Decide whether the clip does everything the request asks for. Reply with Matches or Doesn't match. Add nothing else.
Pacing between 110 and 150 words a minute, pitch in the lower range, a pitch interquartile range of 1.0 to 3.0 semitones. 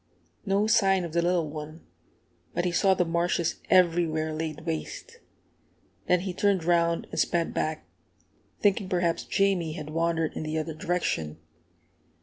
Doesn't match